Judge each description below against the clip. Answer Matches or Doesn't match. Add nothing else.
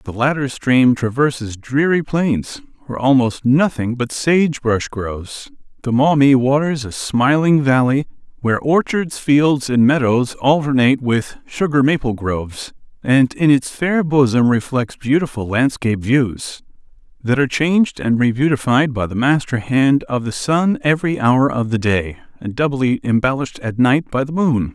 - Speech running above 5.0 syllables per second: Doesn't match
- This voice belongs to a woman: Doesn't match